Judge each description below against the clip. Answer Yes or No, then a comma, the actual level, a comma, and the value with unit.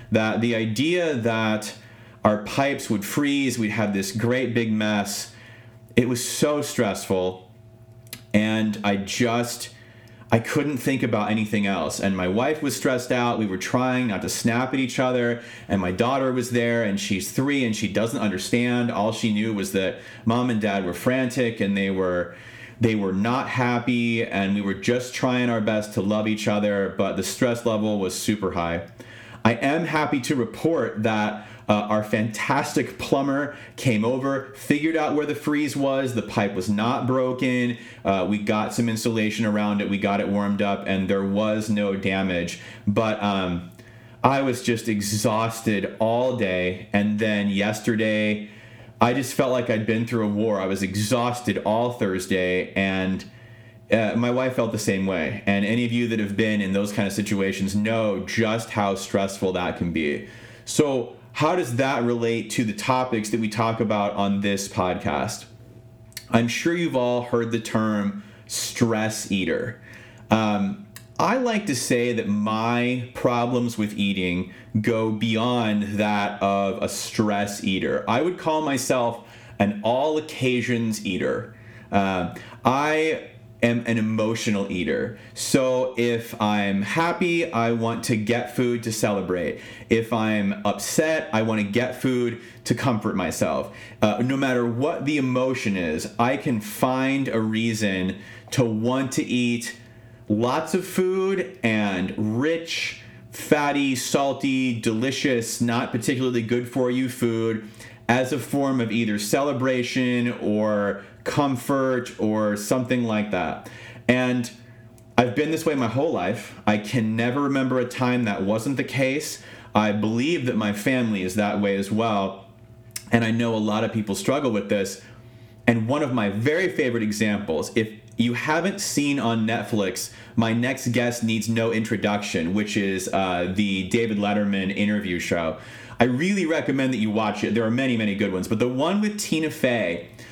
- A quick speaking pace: No, average, 165 wpm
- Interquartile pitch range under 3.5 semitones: Yes, average, 2.9 semitones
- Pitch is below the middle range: Yes, low, 115 Hz